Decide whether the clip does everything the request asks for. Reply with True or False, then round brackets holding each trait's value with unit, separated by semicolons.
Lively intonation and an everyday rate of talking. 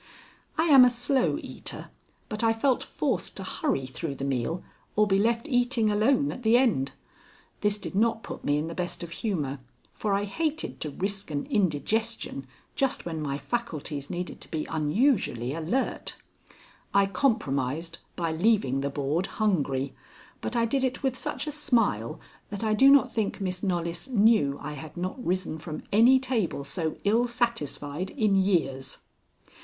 True (7.4 semitones; 170 wpm)